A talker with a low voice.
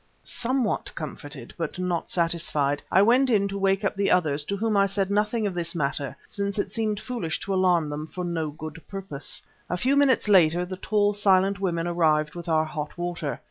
No: medium, 180 Hz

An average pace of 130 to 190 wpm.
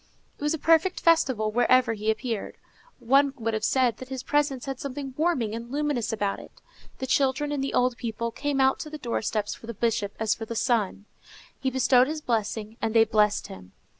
No: fast, 205 wpm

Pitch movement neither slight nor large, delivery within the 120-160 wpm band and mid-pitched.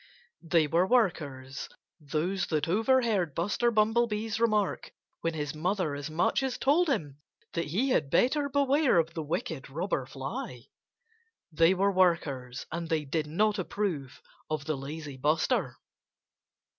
No: wide, 6.0 semitones; average, 140 wpm; medium, 170 Hz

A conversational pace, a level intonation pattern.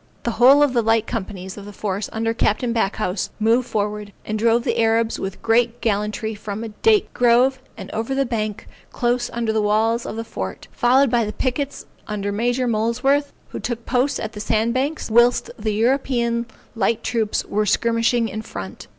Yes: average, 185 wpm; narrow, 2.3 semitones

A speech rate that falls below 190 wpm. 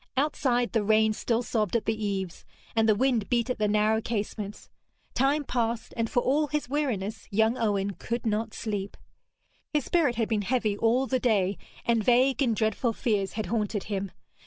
Yes: average, 180 wpm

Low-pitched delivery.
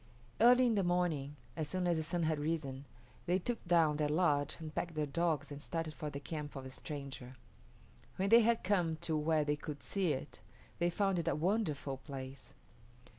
No: medium, 160 Hz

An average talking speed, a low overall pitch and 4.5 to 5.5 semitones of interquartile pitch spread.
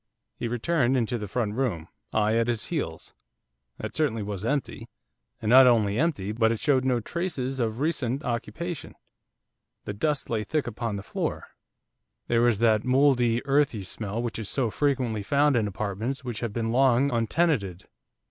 No: average, 165 wpm; low, 120 Hz; average, 3.7 semitones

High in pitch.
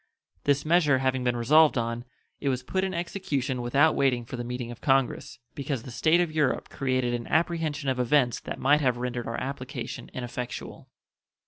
No: low, 130 Hz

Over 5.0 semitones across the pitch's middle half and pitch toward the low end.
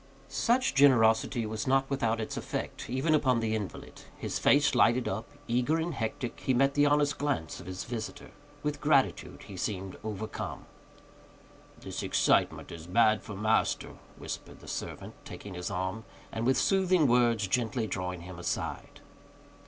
No: average, 4.4 semitones; low, 115 Hz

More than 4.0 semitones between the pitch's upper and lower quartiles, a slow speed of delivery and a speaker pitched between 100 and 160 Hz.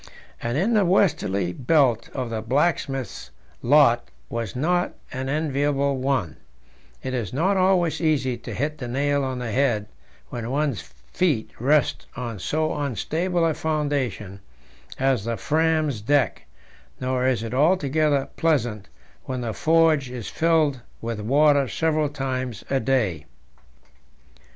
Yes: average, 4.4 semitones; slow, 130 wpm; low, 135 Hz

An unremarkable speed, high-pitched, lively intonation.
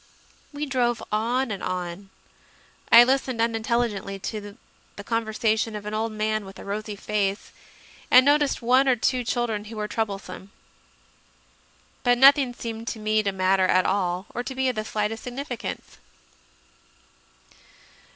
No: average, 145 wpm; high, 220 Hz; average, 3.1 semitones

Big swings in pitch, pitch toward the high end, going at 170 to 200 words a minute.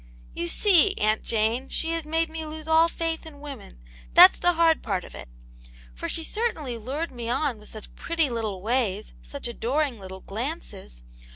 Yes: wide, 7.0 semitones; very high, 270 Hz; average, 185 wpm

